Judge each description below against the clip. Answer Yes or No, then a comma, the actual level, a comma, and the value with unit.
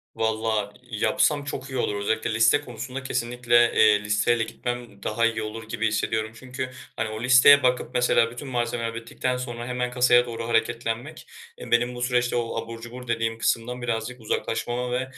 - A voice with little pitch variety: Yes, narrow, 1.7 semitones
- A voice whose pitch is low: Yes, low, 120 Hz